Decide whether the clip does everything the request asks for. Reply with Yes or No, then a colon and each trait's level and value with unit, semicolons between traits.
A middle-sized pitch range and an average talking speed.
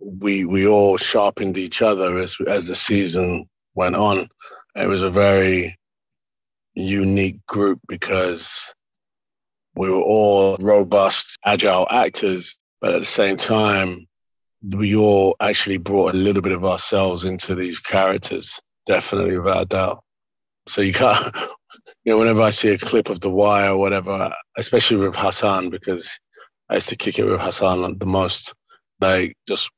No: narrow, 1.4 semitones; average, 155 wpm